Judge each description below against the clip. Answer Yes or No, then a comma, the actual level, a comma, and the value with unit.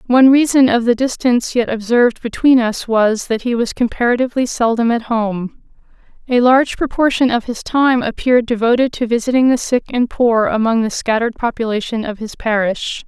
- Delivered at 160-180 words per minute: Yes, average, 175 wpm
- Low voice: No, high, 235 Hz